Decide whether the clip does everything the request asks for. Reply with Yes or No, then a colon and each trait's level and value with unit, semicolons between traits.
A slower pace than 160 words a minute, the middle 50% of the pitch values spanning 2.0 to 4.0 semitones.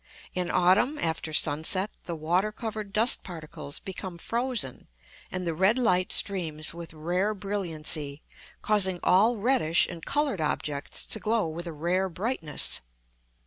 No: average, 140 wpm; average, 4.7 semitones